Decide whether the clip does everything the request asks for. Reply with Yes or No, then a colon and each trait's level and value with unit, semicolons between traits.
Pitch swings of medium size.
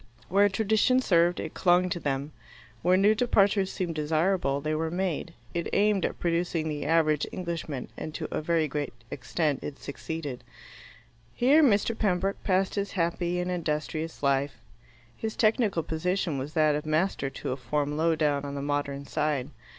Yes: average, 4.1 semitones